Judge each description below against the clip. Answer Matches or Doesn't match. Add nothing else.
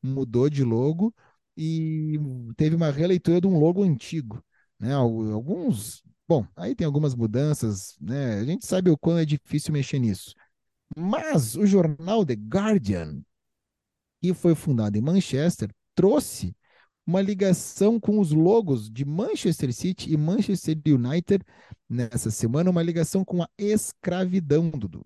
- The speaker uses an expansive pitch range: Matches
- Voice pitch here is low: Doesn't match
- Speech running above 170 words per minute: Doesn't match